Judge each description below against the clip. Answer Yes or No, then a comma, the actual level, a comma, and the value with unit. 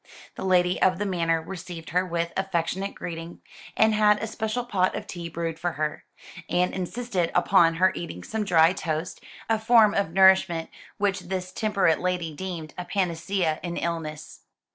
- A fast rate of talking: No, average, 165 wpm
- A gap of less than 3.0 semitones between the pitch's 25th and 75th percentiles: Yes, narrow, 2.6 semitones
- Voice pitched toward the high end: No, medium, 180 Hz